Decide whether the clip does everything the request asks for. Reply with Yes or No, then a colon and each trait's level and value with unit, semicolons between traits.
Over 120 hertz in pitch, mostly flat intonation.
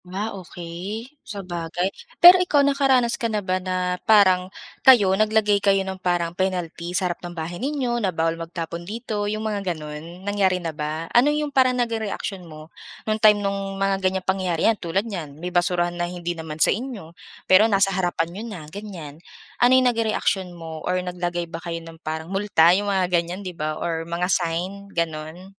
No: medium, 185 Hz; average, 3.4 semitones